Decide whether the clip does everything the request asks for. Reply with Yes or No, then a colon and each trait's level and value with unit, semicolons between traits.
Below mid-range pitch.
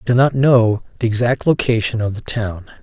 Yes: low, 115 Hz